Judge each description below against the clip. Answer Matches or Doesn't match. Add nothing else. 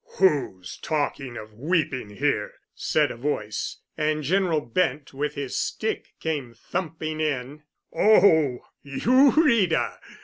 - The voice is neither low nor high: Matches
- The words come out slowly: Matches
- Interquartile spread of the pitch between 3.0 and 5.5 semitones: Matches